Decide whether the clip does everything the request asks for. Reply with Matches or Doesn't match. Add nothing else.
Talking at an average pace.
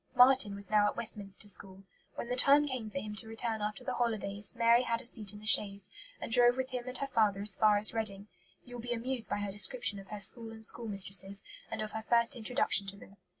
Doesn't match